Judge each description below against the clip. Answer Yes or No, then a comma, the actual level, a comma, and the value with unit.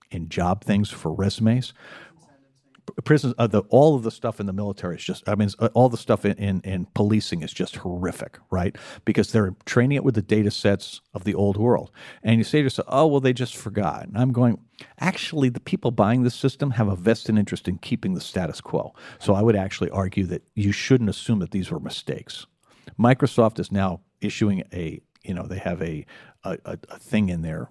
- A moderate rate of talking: No, fast, 215 wpm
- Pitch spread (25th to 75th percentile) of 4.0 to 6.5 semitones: Yes, average, 4.3 semitones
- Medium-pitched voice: No, low, 110 Hz